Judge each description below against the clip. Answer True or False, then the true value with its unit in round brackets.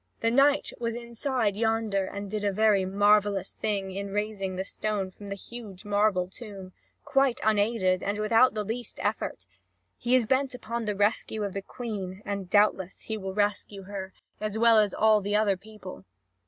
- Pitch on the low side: False (210 Hz)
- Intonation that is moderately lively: False (2.3 semitones)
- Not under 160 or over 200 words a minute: True (180 wpm)